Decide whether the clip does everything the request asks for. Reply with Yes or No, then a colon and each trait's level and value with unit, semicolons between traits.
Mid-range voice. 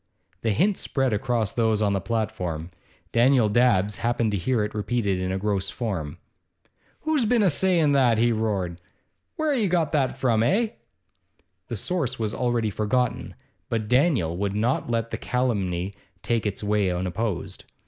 No: low, 115 Hz